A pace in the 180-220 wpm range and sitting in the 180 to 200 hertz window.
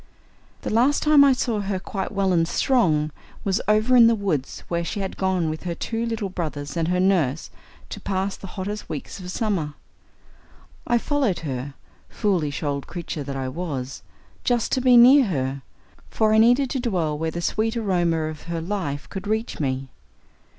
Yes: average, 185 wpm; medium, 185 Hz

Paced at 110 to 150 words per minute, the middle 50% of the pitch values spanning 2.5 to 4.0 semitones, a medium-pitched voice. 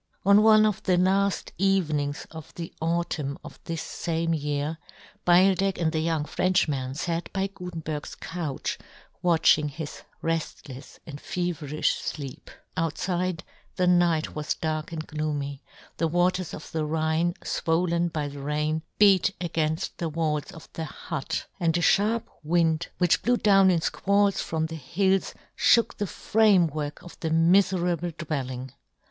Yes: average, 145 wpm; average, 2.8 semitones; medium, 165 Hz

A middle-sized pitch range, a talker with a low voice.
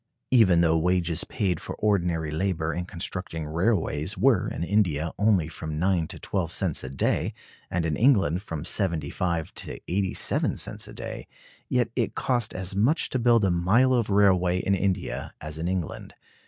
Yes: average, 3.8 semitones; very low, 90 Hz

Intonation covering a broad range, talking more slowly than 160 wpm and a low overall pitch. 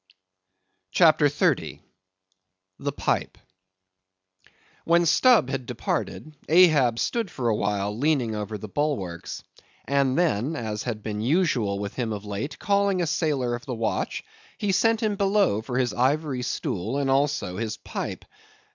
Yes: wide, 6.5 semitones; average, 145 wpm; low, 130 Hz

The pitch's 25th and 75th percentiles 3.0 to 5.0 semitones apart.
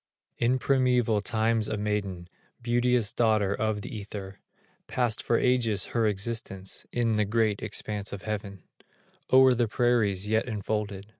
No: narrow, 2.6 semitones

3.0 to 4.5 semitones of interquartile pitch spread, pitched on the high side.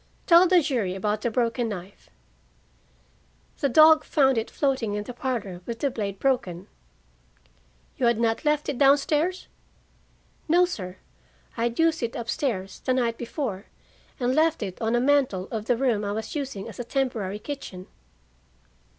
No: average, 5.1 semitones; high, 240 Hz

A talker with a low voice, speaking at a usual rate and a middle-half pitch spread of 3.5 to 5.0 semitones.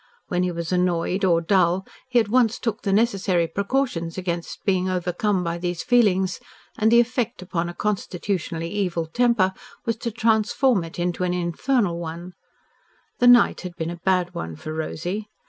No: medium, 185 Hz; average, 170 wpm; average, 4.1 semitones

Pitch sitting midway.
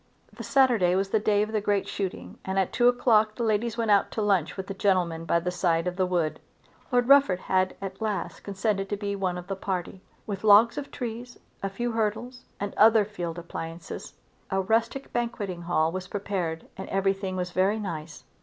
No: high, 195 Hz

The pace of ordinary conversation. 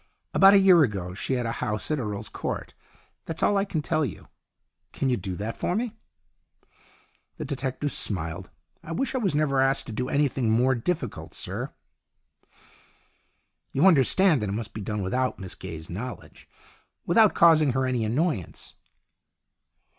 Yes: average, 170 wpm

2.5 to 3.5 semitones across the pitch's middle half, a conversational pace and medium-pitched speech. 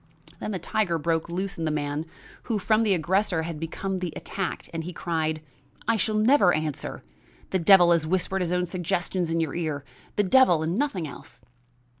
Yes: average, 3.2 semitones; average, 190 wpm; medium, 175 Hz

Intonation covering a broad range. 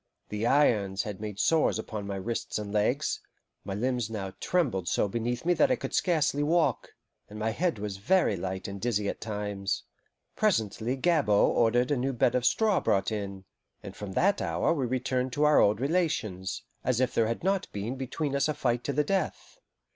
Yes: wide, 6.0 semitones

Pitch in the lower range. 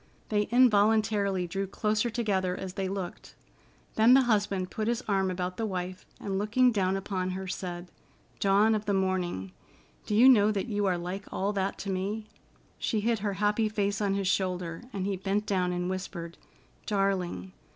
No: high, 195 Hz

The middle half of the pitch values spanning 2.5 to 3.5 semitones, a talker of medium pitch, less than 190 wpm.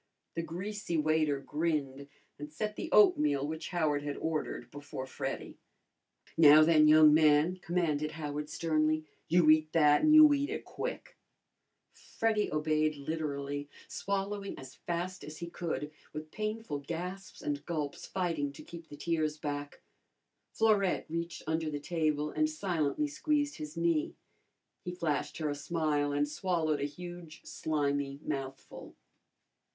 Yes: average, 3.0 semitones; medium, 155 Hz; average, 140 wpm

